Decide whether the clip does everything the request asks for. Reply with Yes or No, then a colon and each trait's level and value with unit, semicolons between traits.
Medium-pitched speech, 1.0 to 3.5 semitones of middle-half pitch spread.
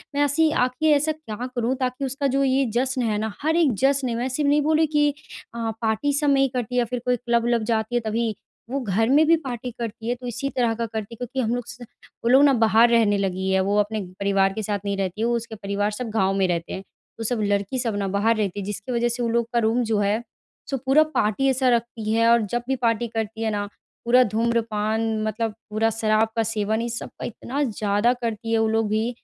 No: high, 230 Hz; average, 2.7 semitones